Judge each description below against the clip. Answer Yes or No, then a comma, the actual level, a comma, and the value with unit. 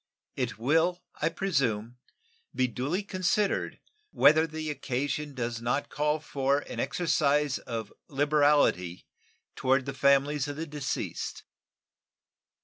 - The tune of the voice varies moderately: Yes, average, 3.0 semitones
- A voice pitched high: No, medium, 145 Hz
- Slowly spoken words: Yes, slow, 115 wpm